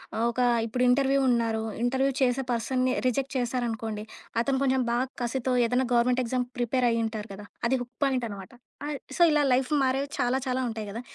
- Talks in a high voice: Yes, very high, 250 Hz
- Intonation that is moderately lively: No, narrow, 2.2 semitones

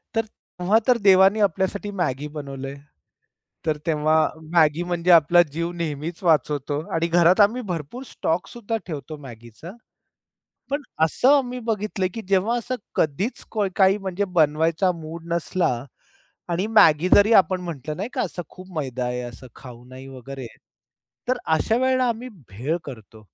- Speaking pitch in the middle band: Yes, medium, 170 Hz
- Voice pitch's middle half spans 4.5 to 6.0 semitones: Yes, wide, 5.5 semitones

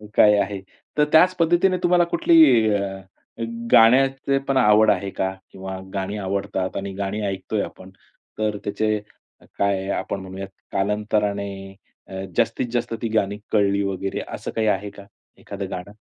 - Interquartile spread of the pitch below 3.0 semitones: Yes, narrow, 2.6 semitones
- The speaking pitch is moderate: No, low, 100 Hz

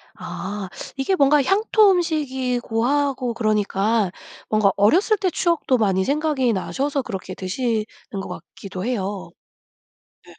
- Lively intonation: Yes, wide, 6.0 semitones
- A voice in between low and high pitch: No, high, 245 Hz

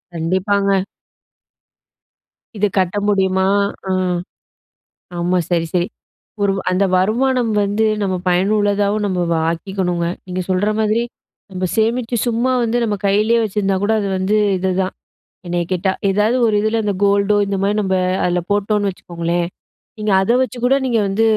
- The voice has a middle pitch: No, high, 200 Hz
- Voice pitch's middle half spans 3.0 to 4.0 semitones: No, narrow, 2.5 semitones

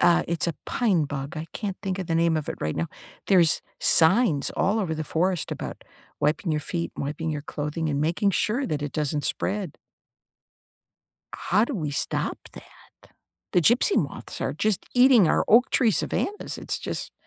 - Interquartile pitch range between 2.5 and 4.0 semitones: No, average, 5.1 semitones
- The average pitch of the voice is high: No, medium, 170 Hz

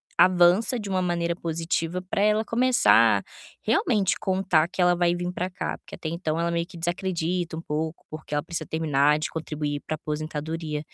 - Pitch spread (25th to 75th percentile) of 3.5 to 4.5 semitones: No, narrow, 2.6 semitones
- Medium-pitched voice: Yes, medium, 170 Hz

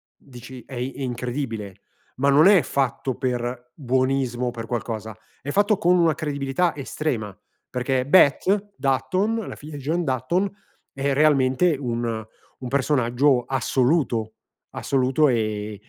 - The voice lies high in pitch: No, low, 130 Hz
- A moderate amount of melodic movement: Yes, average, 3.6 semitones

